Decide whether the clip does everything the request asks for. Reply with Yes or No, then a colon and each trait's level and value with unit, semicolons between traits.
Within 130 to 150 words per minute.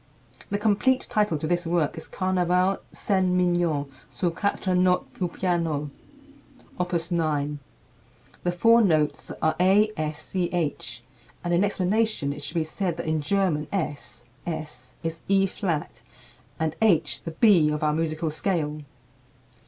Yes: average, 145 wpm